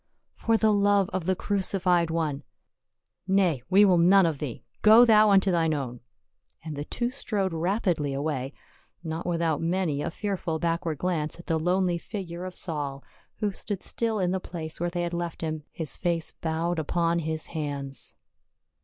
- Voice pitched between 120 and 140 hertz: No, medium, 170 Hz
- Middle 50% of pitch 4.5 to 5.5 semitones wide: No, average, 3.2 semitones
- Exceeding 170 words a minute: Yes, average, 180 wpm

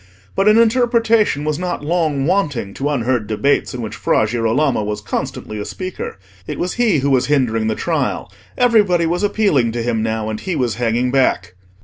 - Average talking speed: Yes, average, 190 wpm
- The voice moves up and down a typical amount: No, wide, 8.2 semitones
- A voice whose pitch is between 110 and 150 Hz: Yes, medium, 140 Hz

